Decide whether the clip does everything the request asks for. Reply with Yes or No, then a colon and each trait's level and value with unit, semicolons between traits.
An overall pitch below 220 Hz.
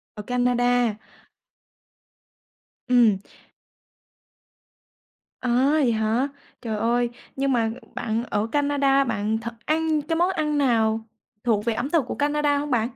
No: high, 245 Hz